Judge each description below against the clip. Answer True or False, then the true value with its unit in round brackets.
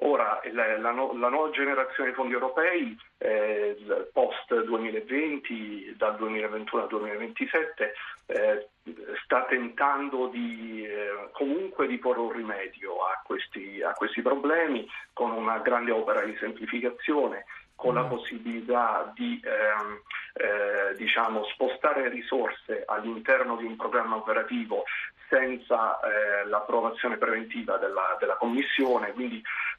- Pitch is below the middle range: True (125 Hz)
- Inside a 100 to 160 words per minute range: True (120 wpm)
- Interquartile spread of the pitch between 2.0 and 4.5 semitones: True (4.2 semitones)